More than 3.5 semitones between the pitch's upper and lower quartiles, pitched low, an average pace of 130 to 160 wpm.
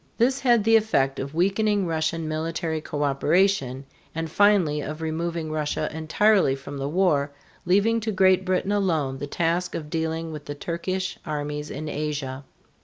No: average, 4.2 semitones; medium, 160 Hz; average, 155 wpm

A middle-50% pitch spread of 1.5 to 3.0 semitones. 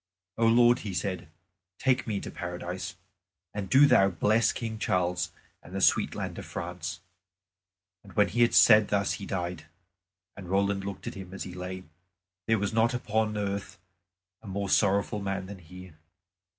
Yes: average, 2.7 semitones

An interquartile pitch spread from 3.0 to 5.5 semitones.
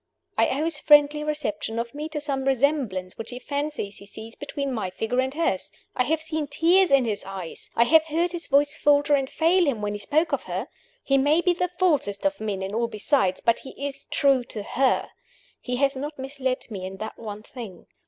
Yes: average, 5.2 semitones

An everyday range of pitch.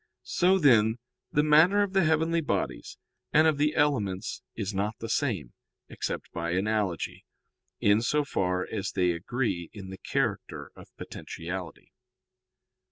No: wide, 8.1 semitones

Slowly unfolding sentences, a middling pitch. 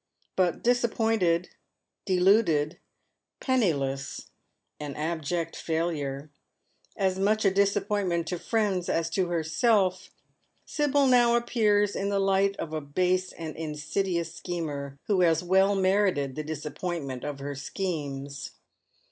Yes: slow, 130 wpm; medium, 180 Hz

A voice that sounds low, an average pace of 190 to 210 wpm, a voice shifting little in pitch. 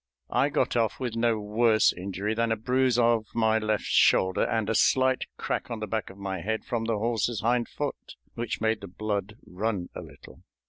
Yes: low, 110 Hz; average, 200 wpm; narrow, 2.0 semitones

